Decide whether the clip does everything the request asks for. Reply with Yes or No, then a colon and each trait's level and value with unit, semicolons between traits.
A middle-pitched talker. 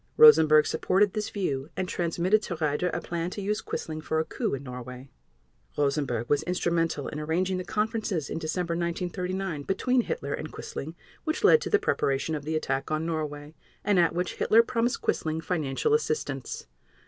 Yes: medium, 165 Hz